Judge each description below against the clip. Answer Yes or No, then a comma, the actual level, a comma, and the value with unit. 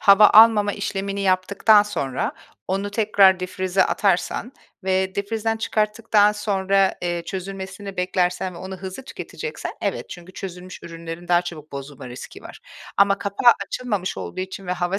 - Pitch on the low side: No, high, 190 Hz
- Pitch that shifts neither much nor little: No, narrow, 2.2 semitones